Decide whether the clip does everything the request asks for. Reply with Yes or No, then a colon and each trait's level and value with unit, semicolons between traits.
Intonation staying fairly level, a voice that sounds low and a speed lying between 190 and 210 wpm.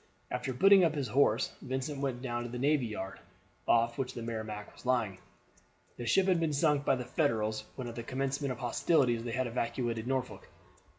No: average, 3.0 semitones; low, 125 Hz; average, 195 wpm